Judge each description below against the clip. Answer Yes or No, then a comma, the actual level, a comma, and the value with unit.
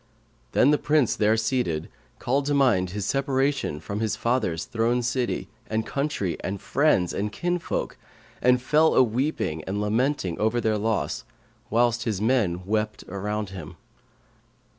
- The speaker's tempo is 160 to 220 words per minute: No, average, 145 wpm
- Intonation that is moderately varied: Yes, average, 4.3 semitones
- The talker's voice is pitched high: No, low, 110 Hz